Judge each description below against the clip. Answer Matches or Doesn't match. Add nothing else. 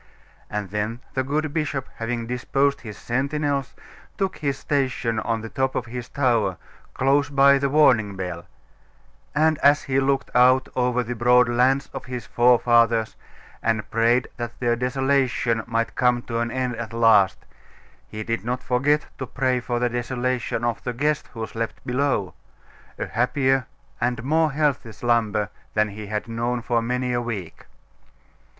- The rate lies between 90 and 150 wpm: Doesn't match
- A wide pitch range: Doesn't match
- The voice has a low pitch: Matches